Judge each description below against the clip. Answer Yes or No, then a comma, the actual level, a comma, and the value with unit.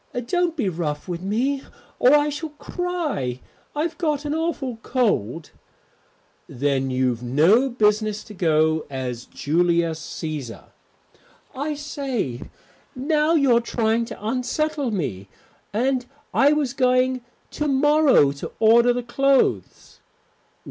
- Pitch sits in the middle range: No, high, 240 Hz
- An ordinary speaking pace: No, slow, 120 wpm